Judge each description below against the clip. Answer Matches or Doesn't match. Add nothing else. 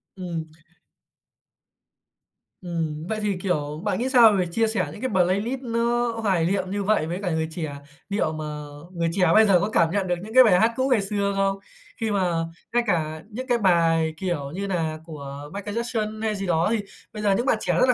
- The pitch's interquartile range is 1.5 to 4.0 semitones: Doesn't match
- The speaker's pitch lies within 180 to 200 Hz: Matches